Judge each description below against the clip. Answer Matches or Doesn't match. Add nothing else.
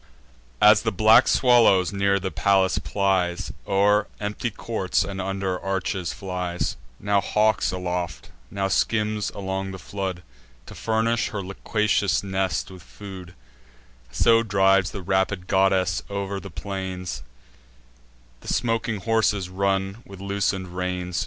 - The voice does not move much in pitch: Matches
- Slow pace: Matches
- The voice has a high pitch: Doesn't match